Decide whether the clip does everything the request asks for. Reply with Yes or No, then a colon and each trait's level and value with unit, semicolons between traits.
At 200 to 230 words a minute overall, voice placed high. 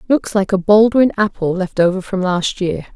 Yes: fast, 205 wpm; high, 195 Hz